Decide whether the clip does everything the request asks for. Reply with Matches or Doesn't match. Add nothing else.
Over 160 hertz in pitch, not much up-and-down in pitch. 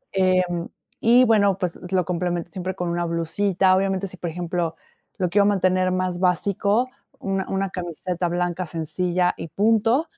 Matches